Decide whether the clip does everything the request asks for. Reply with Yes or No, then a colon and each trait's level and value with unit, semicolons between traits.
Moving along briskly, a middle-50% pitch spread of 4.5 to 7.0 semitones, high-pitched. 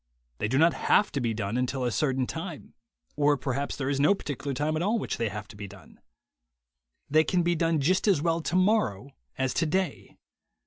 No: fast, 210 wpm; average, 4.9 semitones; medium, 145 Hz